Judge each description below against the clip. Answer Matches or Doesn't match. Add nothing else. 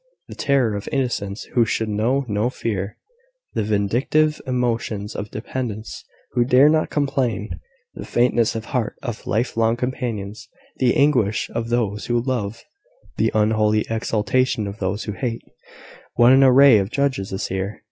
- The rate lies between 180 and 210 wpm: Doesn't match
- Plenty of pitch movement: Doesn't match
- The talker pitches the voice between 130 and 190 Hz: Doesn't match